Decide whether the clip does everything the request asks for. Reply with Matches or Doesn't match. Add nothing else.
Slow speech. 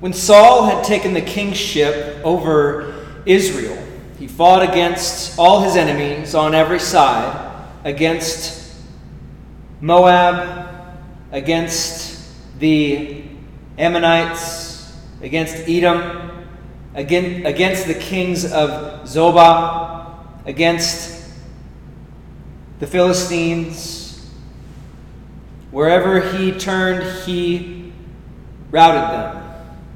Matches